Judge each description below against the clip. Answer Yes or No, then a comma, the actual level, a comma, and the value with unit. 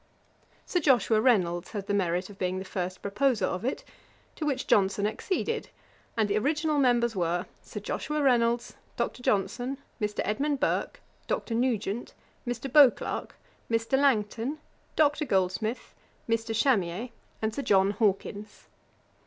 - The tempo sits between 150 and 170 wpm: No, slow, 135 wpm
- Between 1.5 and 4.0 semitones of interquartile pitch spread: No, average, 4.9 semitones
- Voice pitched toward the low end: No, high, 225 Hz